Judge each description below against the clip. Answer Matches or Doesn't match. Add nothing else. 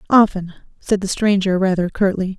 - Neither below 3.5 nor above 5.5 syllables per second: Matches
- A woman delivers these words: Matches